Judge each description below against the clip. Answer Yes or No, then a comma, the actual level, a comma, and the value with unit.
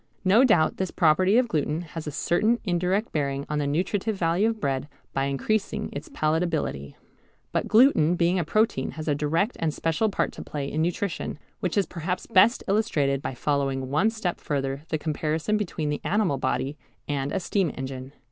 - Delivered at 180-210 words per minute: Yes, average, 185 wpm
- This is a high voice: No, medium, 160 Hz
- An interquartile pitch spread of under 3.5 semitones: No, average, 5.2 semitones